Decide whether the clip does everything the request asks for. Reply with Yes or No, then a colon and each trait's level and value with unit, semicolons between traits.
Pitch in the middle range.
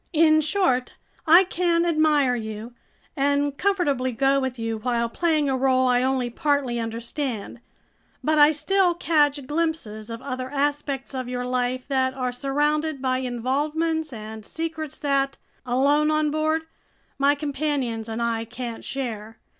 No: very high, 275 Hz